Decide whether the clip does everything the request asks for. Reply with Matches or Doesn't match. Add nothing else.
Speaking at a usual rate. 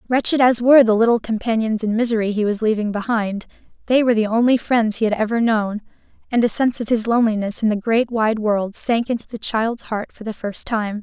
Doesn't match